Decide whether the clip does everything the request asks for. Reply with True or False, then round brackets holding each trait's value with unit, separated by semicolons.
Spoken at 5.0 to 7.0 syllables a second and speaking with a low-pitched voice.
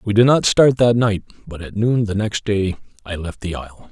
True (5.2 syllables/s; 105 Hz)